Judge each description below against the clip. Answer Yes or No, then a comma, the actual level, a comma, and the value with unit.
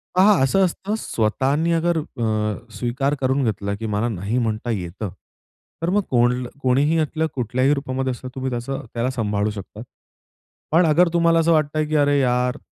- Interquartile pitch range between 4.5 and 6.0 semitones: Yes, average, 5.1 semitones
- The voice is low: Yes, low, 130 Hz